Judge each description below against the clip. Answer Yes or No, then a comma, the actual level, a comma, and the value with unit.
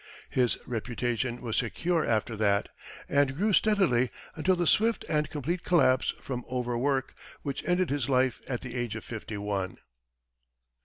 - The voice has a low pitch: Yes, low, 130 Hz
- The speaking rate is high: No, average, 155 wpm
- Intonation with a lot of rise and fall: No, average, 4.6 semitones